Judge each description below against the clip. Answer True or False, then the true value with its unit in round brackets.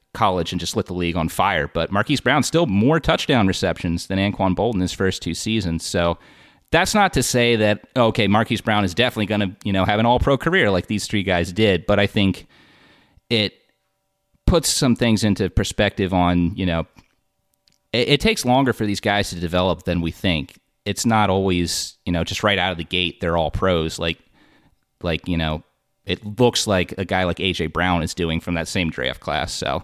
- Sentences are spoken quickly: True (210 wpm)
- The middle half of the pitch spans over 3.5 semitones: True (3.9 semitones)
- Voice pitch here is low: True (95 Hz)